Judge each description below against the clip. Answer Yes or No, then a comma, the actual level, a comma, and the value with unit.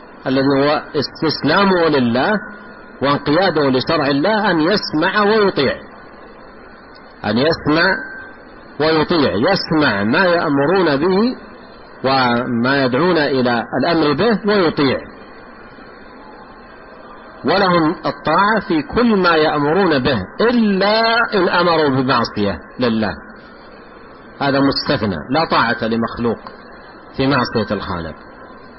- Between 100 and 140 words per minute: No, average, 90 wpm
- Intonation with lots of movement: Yes, wide, 7.7 semitones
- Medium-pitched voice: Yes, medium, 145 Hz